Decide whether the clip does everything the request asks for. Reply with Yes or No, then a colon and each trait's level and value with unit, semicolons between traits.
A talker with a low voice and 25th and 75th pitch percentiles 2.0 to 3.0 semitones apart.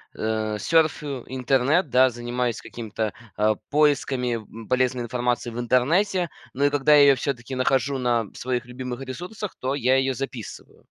Yes: low, 130 Hz; narrow, 2.6 semitones